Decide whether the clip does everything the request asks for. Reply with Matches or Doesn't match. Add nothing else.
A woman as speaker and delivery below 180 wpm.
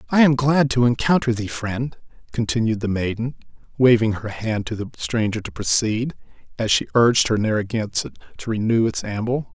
Doesn't match